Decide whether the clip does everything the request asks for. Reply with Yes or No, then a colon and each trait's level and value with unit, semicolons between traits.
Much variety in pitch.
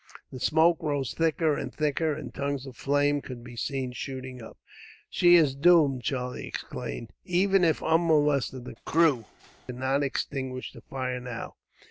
No: average, 3.7 semitones